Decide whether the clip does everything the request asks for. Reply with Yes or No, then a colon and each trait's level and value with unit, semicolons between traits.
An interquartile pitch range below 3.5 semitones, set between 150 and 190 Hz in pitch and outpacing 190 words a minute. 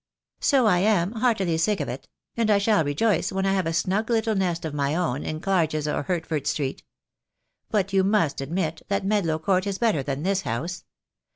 No: average, 4.4 semitones; medium, 185 Hz; fast, 205 wpm